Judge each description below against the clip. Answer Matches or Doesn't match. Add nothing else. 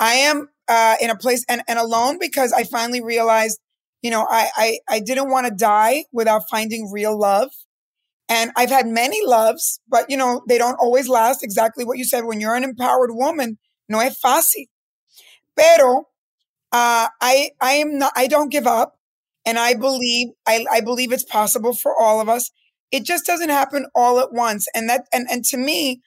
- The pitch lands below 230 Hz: Doesn't match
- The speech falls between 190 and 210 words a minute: Matches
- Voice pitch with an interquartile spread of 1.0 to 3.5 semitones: Matches